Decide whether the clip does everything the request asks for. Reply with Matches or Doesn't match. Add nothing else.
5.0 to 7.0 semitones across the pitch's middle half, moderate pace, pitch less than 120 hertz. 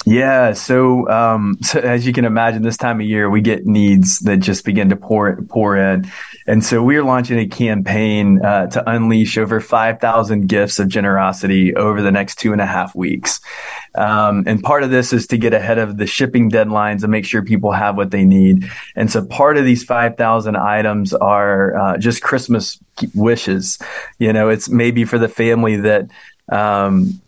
Doesn't match